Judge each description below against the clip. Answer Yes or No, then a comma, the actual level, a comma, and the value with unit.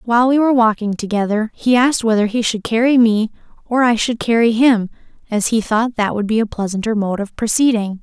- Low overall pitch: No, high, 225 Hz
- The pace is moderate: No, fast, 210 wpm